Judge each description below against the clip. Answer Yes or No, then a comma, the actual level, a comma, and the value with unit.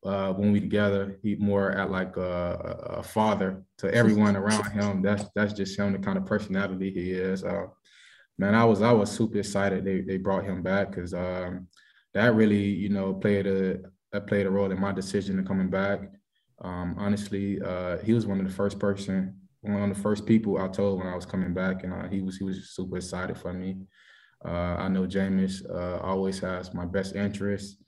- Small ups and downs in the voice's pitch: Yes, narrow, 1.3 semitones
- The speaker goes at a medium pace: No, fast, 210 wpm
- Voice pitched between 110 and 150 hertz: No, very low, 95 Hz